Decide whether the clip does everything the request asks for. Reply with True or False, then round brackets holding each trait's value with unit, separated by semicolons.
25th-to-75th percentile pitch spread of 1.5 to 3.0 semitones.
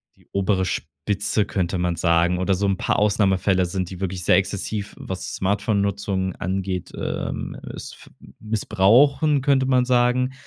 True (2.7 semitones)